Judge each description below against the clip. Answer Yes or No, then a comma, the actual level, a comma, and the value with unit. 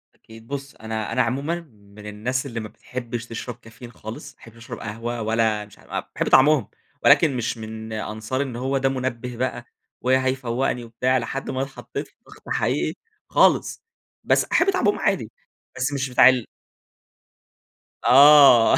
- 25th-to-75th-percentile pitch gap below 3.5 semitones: Yes, average, 2.8 semitones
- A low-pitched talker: Yes, low, 120 Hz